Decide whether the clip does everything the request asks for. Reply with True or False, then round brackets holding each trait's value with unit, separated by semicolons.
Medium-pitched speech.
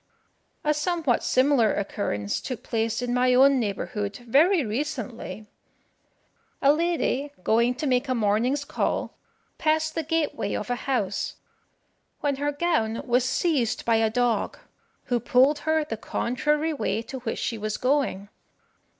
False (250 Hz)